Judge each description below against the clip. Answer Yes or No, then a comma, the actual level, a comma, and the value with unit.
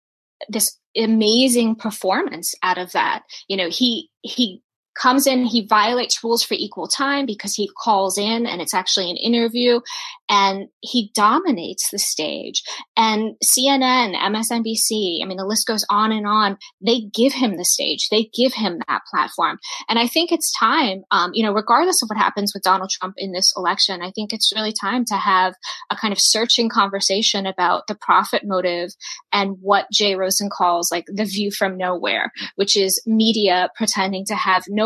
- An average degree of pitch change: Yes, average, 3.4 semitones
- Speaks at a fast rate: No, average, 180 wpm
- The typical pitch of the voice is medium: No, high, 215 Hz